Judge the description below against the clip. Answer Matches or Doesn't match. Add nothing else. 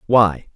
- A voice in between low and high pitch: Doesn't match